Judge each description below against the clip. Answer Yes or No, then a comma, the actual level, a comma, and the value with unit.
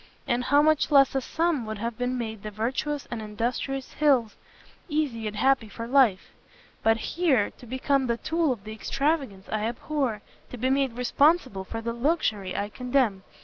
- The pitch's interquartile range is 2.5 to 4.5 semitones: Yes, average, 4.2 semitones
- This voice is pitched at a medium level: No, high, 245 Hz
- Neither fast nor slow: Yes, average, 175 wpm